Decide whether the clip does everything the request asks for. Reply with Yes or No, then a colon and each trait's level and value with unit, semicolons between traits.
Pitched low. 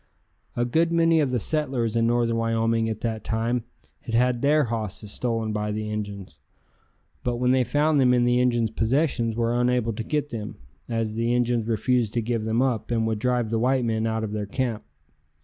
Yes: low, 115 Hz